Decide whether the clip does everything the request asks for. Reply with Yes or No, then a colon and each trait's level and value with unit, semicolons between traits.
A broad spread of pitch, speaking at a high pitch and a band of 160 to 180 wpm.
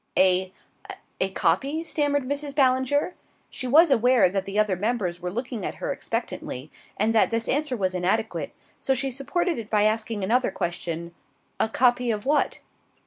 Yes: wide, 5.7 semitones; high, 230 Hz; average, 165 wpm